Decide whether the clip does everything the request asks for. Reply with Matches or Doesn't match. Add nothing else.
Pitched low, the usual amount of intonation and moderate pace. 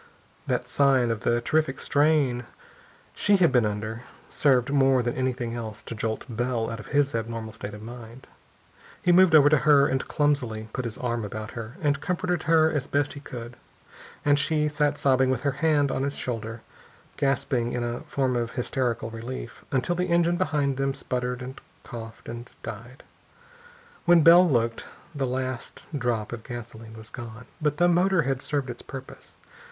Matches